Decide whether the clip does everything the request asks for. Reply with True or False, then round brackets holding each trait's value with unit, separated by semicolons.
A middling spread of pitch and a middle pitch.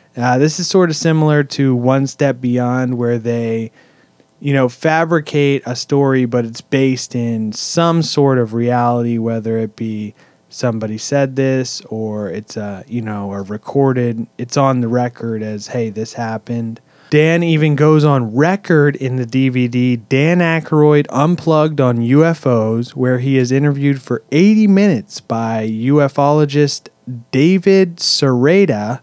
False (4.0 semitones; 130 Hz)